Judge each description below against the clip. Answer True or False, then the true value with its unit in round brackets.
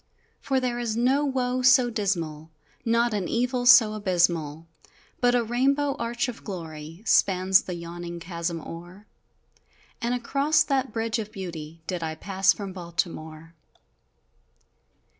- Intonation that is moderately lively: False (6.3 semitones)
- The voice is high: True (205 Hz)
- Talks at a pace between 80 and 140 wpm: True (135 wpm)